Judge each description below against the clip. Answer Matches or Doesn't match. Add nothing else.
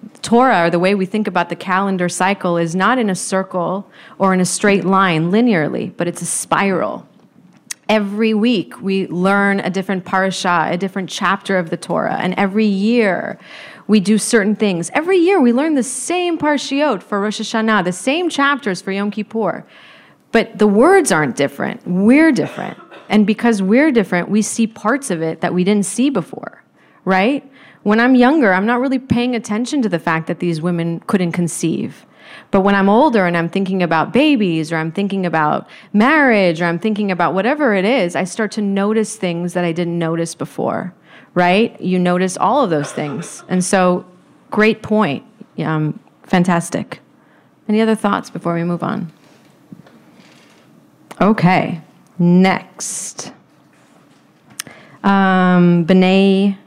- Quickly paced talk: Doesn't match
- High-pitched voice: Matches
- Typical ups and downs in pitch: Matches